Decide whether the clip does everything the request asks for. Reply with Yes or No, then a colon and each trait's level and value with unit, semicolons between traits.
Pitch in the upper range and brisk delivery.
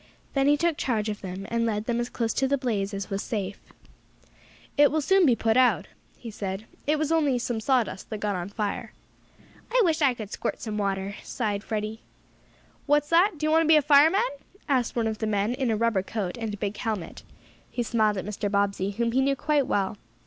Yes: high, 230 Hz; fast, 220 wpm